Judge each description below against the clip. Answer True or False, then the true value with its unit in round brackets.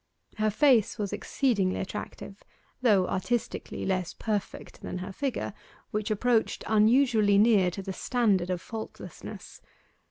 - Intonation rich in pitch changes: False (3.4 semitones)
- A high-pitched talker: True (210 Hz)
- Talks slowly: True (125 wpm)